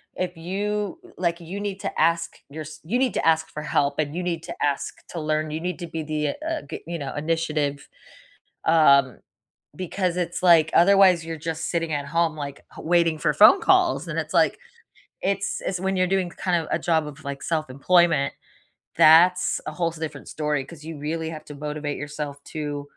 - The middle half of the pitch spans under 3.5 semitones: Yes, average, 2.8 semitones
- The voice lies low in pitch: No, medium, 160 Hz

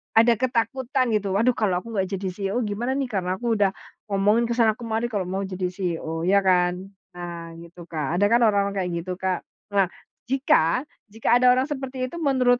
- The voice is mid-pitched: No, high, 205 Hz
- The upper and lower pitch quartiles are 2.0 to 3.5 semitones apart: No, average, 4.7 semitones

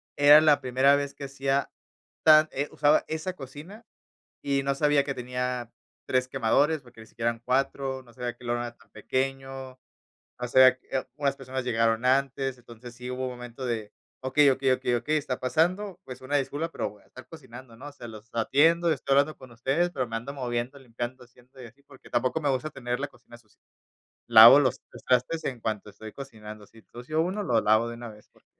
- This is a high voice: No, low, 130 Hz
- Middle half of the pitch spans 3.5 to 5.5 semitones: No, average, 2.9 semitones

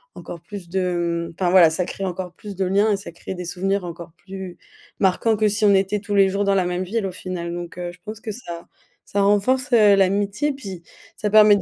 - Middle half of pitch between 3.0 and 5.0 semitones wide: No, narrow, 2.5 semitones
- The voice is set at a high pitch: Yes, high, 195 Hz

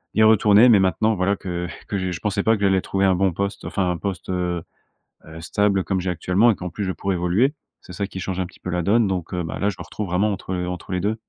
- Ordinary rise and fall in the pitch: No, narrow, 2.2 semitones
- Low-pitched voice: Yes, very low, 95 Hz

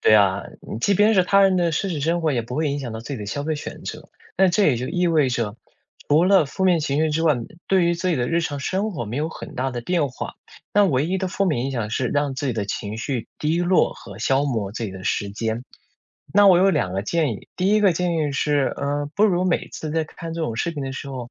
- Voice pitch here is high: No, medium, 150 Hz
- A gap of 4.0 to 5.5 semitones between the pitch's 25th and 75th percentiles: No, wide, 6.3 semitones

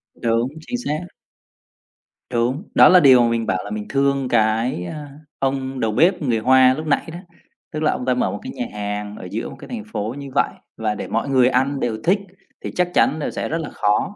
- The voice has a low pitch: Yes, low, 130 Hz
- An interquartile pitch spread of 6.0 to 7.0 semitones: No, average, 4.8 semitones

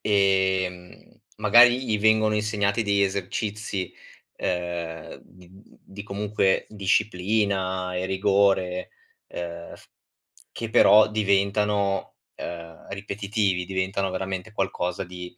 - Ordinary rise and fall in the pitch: No, narrow, 2.3 semitones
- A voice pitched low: Yes, very low, 95 Hz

